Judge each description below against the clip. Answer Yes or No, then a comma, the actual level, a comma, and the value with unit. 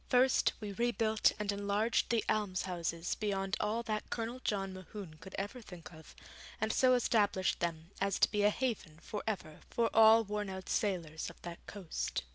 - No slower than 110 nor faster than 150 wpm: No, average, 175 wpm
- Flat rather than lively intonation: No, average, 3.0 semitones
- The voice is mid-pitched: No, high, 205 Hz